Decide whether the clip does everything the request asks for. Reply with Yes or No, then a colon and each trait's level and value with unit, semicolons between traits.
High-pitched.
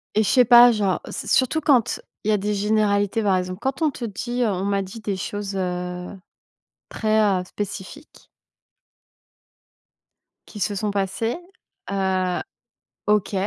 Yes: high, 205 Hz